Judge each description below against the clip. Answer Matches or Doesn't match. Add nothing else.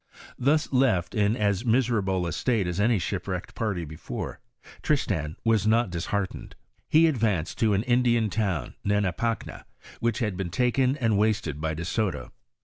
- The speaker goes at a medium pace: Matches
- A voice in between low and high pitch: Doesn't match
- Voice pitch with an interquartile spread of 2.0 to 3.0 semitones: Doesn't match